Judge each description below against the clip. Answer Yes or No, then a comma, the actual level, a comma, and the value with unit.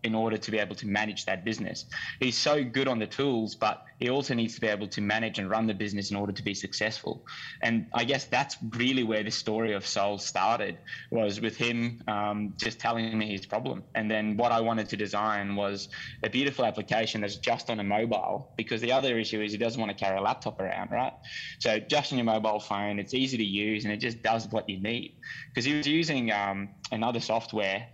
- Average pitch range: No, narrow, 2.0 semitones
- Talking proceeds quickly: Yes, fast, 230 wpm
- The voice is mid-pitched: No, low, 110 Hz